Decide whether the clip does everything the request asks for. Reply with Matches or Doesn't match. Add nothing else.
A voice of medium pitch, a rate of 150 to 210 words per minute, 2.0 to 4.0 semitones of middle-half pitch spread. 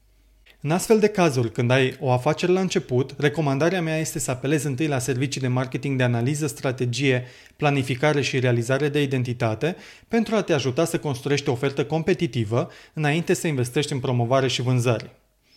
Matches